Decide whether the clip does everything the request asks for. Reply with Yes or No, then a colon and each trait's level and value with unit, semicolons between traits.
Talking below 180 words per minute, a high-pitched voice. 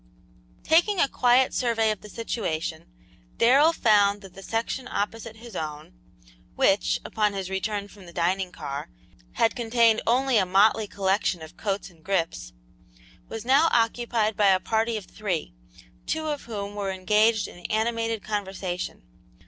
Yes: average, 150 wpm; high, 215 Hz